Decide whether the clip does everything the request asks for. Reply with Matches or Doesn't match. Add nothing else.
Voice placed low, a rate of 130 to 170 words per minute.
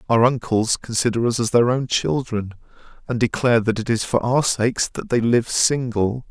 Doesn't match